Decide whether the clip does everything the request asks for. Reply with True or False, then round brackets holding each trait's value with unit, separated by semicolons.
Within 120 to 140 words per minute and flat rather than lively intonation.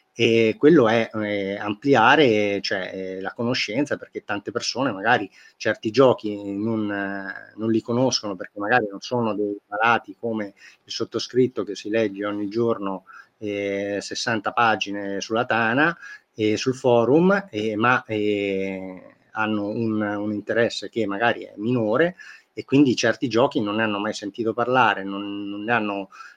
False (155 wpm; 2.3 semitones)